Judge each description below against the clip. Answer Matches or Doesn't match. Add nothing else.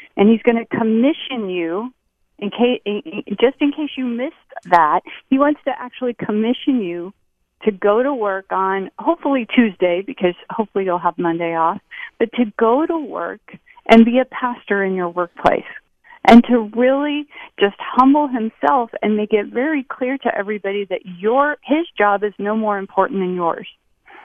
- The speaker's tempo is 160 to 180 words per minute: Matches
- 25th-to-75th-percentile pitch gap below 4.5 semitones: Doesn't match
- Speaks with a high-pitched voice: Matches